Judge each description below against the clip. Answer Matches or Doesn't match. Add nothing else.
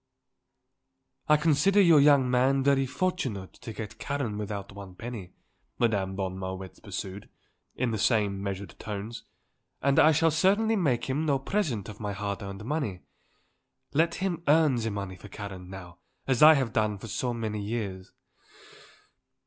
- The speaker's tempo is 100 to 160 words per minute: Matches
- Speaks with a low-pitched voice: Matches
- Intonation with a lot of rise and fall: Matches